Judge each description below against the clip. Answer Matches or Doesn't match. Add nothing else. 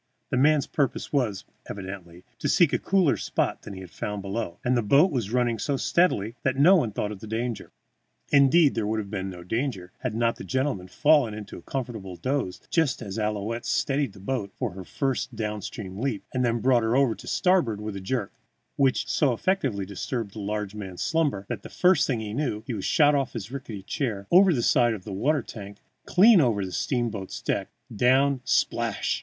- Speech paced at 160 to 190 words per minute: Doesn't match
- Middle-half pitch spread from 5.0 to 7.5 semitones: Matches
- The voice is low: Matches